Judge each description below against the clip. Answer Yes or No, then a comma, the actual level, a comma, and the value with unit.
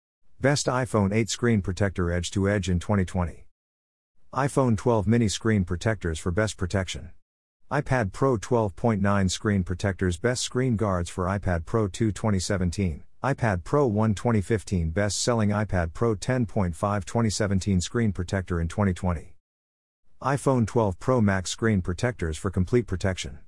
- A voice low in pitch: Yes, low, 100 Hz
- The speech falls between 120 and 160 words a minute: Yes, average, 140 wpm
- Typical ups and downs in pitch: Yes, average, 4.1 semitones